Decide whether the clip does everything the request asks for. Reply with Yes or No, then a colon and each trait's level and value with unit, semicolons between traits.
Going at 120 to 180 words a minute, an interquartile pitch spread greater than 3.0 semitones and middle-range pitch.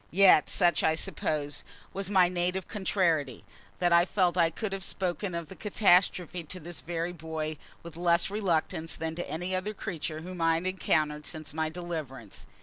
No: average, 175 wpm; average, 2.7 semitones; medium, 175 Hz